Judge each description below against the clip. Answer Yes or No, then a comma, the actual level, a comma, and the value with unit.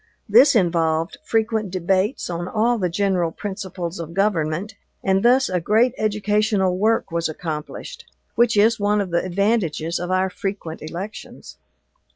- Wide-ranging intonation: No, average, 3.8 semitones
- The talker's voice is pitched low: No, high, 190 Hz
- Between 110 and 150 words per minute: Yes, average, 145 wpm